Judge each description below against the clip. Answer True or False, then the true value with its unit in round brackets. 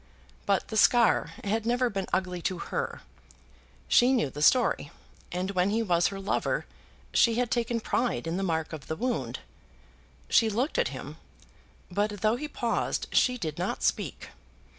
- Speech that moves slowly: False (165 wpm)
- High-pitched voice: True (210 Hz)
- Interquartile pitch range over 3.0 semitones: True (4.8 semitones)